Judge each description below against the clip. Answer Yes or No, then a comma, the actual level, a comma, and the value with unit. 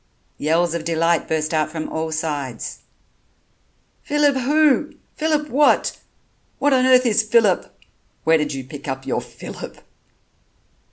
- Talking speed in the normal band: No, slow, 130 wpm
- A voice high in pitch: No, medium, 170 Hz